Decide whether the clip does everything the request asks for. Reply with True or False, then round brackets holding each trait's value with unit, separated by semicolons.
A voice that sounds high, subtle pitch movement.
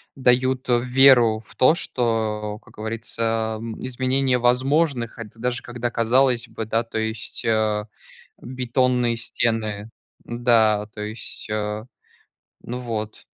False (115 Hz; 2.2 semitones)